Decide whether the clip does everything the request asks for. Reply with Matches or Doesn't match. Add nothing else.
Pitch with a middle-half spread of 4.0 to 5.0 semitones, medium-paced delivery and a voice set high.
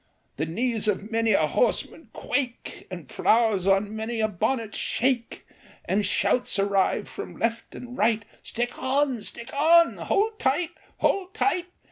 Matches